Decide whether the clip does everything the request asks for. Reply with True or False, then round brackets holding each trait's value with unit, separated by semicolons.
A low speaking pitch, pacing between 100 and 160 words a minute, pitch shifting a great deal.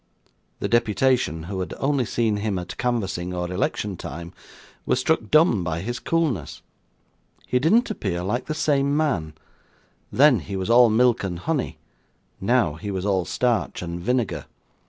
True (105 Hz; 155 wpm; 6.0 semitones)